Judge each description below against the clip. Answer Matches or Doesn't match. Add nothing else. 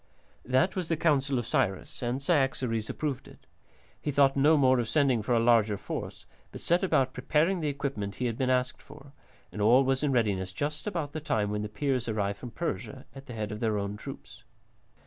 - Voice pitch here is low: Matches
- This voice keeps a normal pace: Doesn't match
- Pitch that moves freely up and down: Doesn't match